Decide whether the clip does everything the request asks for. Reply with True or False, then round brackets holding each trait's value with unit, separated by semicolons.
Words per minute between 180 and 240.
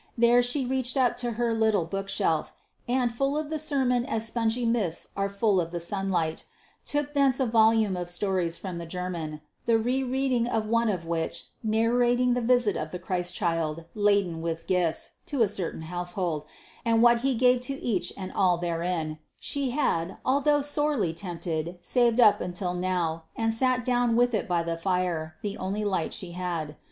True (185 wpm)